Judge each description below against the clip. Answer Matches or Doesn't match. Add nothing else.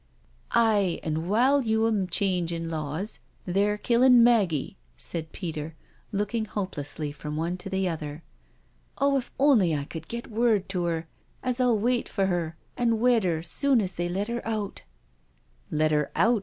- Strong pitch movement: Matches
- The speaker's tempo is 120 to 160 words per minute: Doesn't match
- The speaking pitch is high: Matches